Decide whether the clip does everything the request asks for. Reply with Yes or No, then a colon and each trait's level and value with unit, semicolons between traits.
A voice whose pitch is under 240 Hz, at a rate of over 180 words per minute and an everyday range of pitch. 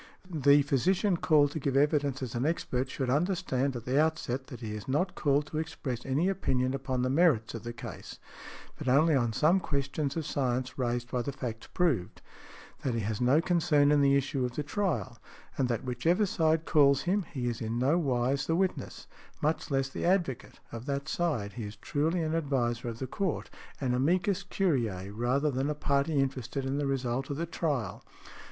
Yes: medium, 140 Hz; average, 195 wpm; average, 4.0 semitones